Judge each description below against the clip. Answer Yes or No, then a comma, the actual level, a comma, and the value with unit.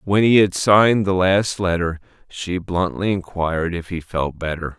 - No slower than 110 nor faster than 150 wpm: No, average, 175 wpm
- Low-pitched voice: Yes, very low, 90 Hz